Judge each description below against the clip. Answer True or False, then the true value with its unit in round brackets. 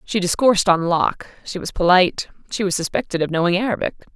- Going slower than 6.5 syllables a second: False (6.6 syllables/s)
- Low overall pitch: False (185 Hz)